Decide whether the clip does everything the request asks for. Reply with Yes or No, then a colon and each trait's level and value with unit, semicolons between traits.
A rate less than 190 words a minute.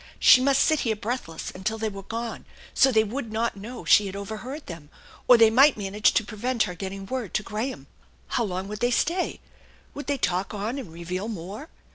No: fast, 205 wpm